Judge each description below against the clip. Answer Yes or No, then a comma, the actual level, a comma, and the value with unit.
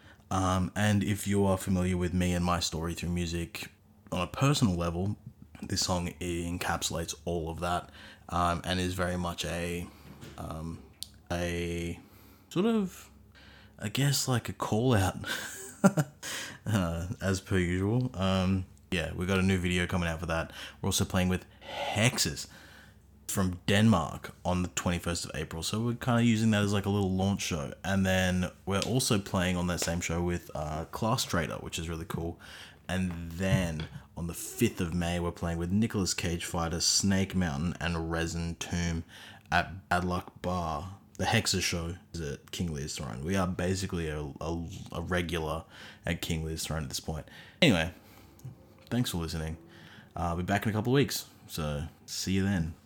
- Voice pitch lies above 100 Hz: No, very low, 90 Hz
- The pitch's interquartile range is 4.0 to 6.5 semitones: No, average, 2.9 semitones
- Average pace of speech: Yes, average, 180 wpm